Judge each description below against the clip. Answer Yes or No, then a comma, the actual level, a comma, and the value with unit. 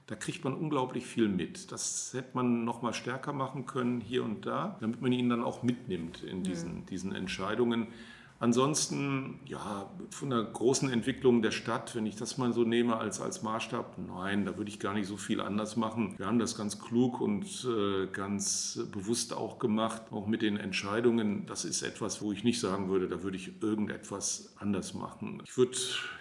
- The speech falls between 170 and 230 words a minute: Yes, fast, 190 wpm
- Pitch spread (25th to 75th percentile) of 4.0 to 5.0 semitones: No, average, 3.0 semitones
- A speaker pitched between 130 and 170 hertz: No, low, 115 Hz